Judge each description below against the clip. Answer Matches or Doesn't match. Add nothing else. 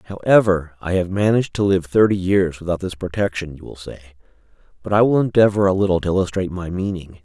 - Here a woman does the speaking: Doesn't match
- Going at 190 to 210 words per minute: Matches